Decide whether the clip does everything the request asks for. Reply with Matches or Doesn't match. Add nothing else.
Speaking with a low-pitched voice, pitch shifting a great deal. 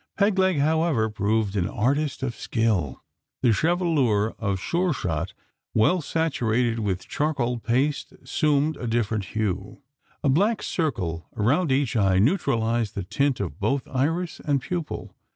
Matches